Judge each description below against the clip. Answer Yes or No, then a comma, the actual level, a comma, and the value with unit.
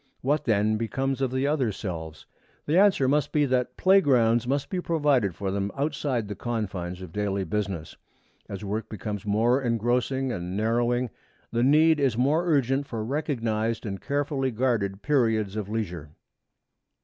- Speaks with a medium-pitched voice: No, low, 120 Hz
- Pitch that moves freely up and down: No, average, 4.8 semitones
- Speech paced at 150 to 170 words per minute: Yes, average, 155 wpm